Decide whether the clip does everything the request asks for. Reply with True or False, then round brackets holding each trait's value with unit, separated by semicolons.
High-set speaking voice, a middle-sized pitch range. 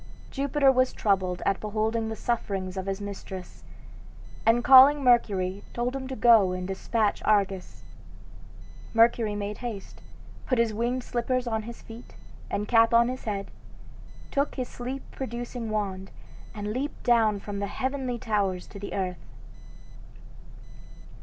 True (225 Hz; 3.5 semitones)